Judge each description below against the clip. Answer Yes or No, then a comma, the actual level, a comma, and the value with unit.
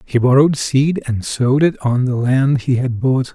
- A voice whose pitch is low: Yes, low, 130 Hz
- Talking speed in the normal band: No, fast, 215 wpm